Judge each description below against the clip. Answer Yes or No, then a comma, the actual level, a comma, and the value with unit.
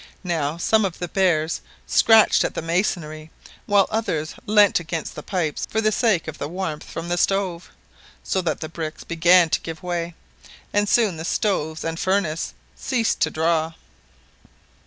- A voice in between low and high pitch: Yes, medium, 170 Hz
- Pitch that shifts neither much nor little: Yes, average, 3.6 semitones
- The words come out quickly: No, average, 165 wpm